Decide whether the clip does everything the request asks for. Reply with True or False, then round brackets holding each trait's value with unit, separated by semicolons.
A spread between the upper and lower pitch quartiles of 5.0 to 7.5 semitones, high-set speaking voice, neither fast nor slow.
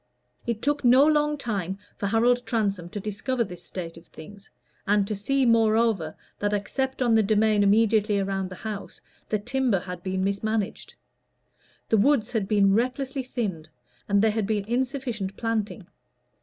False (3.5 semitones; 215 Hz; 160 wpm)